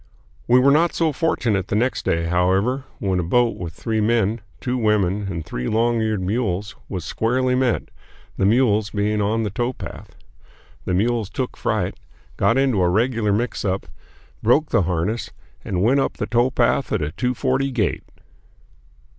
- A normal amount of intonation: Yes, average, 4.3 semitones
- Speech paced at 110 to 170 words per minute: Yes, average, 165 wpm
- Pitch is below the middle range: Yes, low, 110 Hz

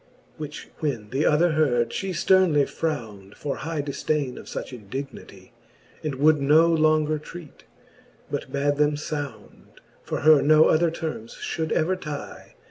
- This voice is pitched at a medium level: Yes, medium, 150 Hz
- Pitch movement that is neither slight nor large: No, narrow, 2.1 semitones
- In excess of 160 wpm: No, average, 145 wpm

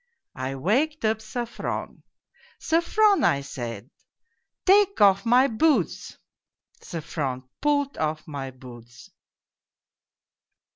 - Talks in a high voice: Yes, high, 200 Hz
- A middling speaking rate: No, slow, 105 wpm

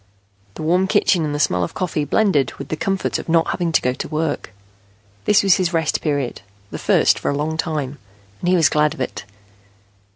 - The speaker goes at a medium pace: No, fast, 215 wpm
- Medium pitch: Yes, medium, 155 Hz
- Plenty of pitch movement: No, average, 3.4 semitones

